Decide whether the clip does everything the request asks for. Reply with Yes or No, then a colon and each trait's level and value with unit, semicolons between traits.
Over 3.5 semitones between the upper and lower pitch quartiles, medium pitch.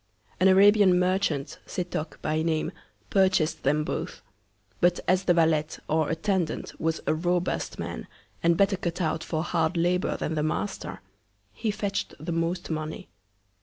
No: average, 2.7 semitones; medium, 170 Hz